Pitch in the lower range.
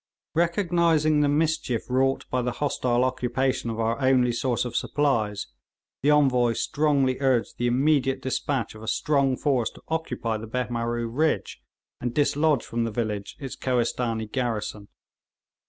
Yes: low, 125 Hz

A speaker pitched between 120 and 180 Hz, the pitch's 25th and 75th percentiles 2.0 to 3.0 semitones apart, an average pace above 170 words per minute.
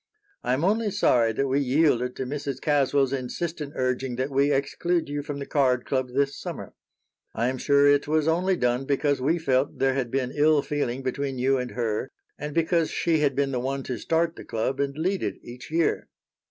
Yes: medium, 140 Hz; narrow, 2.6 semitones; fast, 205 wpm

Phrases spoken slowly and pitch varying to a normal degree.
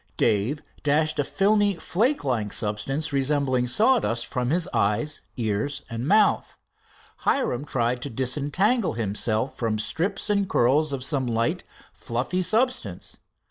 No: slow, 125 wpm; wide, 7.1 semitones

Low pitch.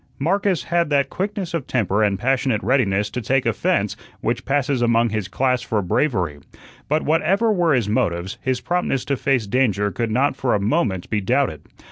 Yes: low, 125 Hz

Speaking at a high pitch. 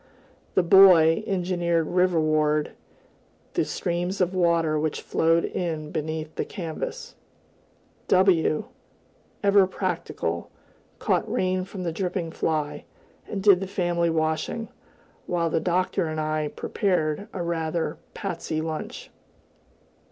No: medium, 170 Hz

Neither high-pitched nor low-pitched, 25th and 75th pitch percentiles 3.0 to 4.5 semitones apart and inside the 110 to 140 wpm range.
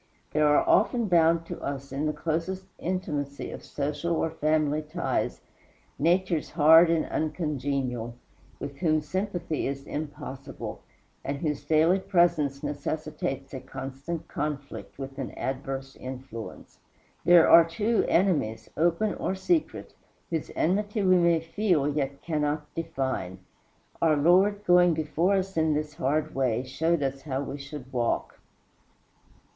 Yes: medium, 155 Hz; average, 3.6 semitones; slow, 135 wpm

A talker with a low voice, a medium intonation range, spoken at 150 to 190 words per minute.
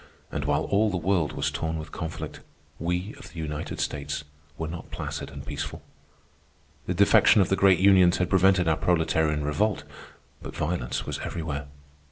Yes: very low, 85 Hz; average, 3.3 semitones; average, 170 wpm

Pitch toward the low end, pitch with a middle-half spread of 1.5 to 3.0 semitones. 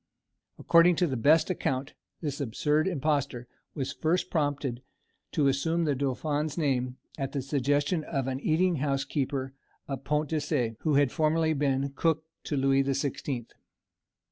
No: medium, 145 Hz; narrow, 2.6 semitones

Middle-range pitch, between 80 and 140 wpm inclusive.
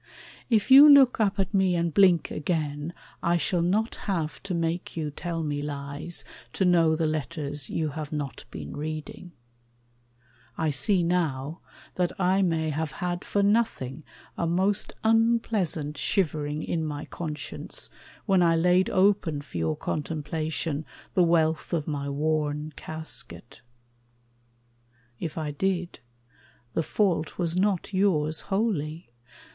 Yes: medium, 165 Hz; slow, 135 wpm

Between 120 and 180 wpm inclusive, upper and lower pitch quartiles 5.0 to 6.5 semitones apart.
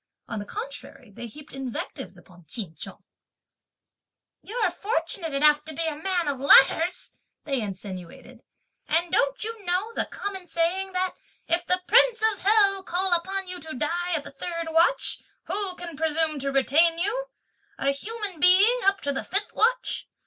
Yes: average, 165 wpm; wide, 5.4 semitones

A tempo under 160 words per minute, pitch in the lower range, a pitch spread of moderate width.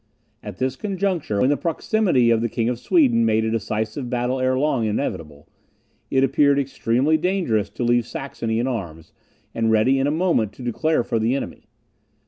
No: average, 180 wpm; low, 125 Hz; average, 4.1 semitones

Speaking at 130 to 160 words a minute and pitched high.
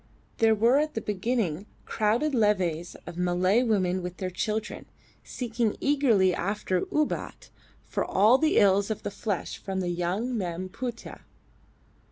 Yes: average, 145 wpm; high, 205 Hz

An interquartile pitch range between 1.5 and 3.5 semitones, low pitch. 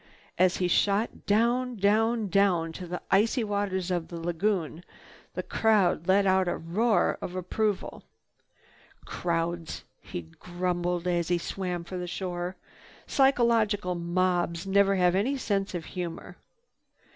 No: average, 2.8 semitones; medium, 185 Hz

